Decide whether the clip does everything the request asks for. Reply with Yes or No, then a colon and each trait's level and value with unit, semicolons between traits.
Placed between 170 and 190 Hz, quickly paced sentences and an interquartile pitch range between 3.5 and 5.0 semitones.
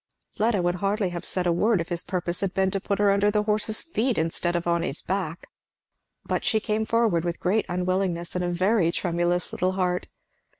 No: medium, 185 Hz; fast, 210 wpm; average, 3.0 semitones